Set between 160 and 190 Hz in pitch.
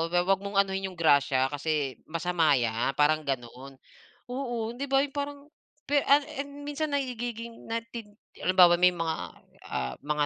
Yes: medium, 185 Hz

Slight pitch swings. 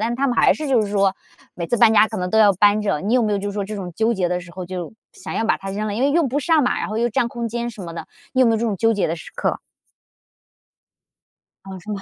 No: average, 3.5 semitones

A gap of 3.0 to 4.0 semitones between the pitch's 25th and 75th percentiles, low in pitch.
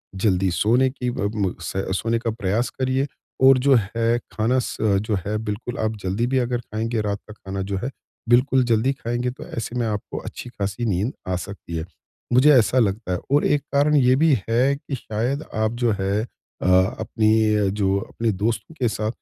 Yes: average, 3.4 semitones; low, 115 Hz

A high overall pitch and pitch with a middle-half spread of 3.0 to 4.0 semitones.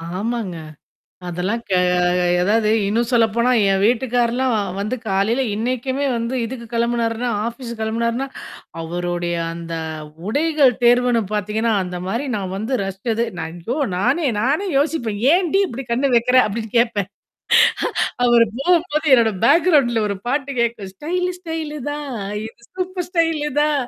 No: high, 235 Hz; average, 4.5 semitones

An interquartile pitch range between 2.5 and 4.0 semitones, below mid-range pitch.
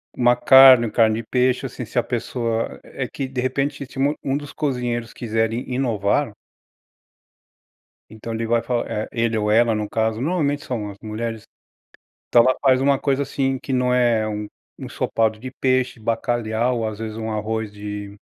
Yes: average, 2.8 semitones; low, 120 Hz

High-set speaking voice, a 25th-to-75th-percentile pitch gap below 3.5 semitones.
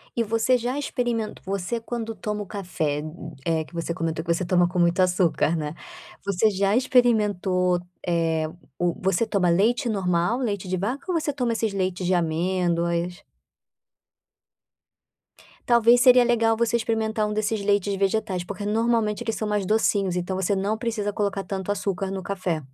No: high, 200 Hz; average, 3.9 semitones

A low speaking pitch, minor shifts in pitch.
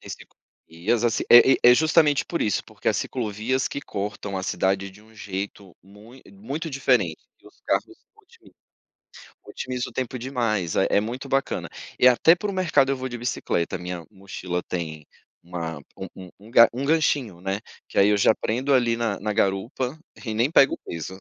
No: low, 115 Hz; average, 5.3 semitones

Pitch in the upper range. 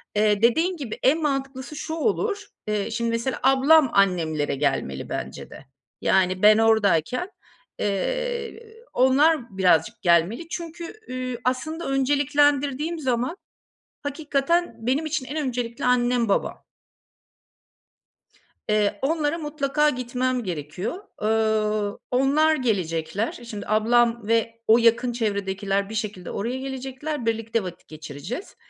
Yes: high, 245 Hz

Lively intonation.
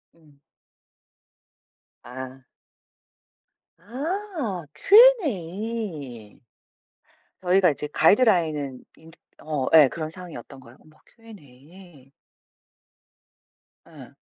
Yes: wide, 7.2 semitones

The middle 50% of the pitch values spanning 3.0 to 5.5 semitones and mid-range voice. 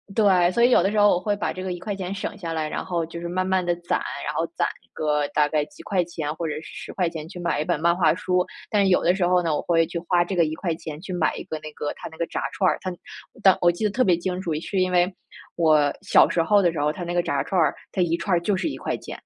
No: narrow, 2.4 semitones; medium, 175 Hz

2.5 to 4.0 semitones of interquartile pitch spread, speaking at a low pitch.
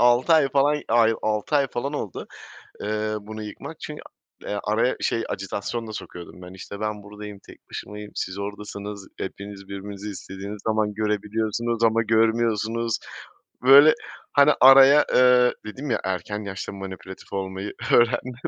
Yes: average, 2.8 semitones; low, 110 Hz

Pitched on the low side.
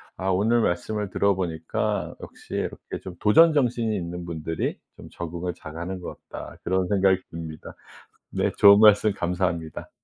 Yes: very low, 95 Hz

